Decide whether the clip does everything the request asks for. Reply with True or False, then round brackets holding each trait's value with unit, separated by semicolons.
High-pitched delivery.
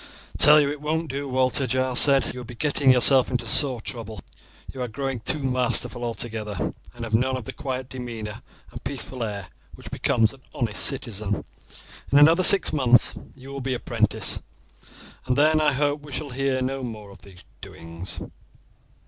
False (130 Hz)